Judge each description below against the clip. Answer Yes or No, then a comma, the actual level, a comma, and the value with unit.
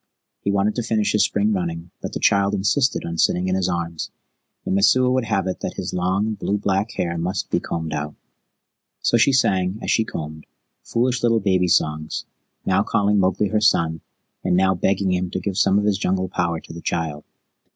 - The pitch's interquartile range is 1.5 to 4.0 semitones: Yes, average, 3.1 semitones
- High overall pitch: No, very low, 95 Hz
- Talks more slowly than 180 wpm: No, fast, 205 wpm